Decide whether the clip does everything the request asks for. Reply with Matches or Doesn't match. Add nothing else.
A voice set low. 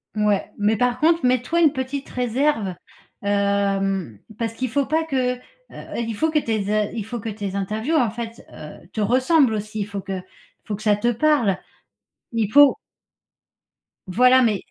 Doesn't match